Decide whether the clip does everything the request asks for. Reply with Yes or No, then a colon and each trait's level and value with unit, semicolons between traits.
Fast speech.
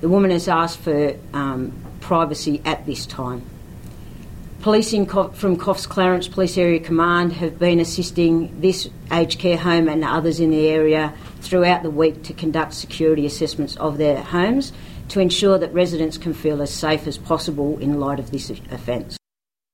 Yes: fast, 165 wpm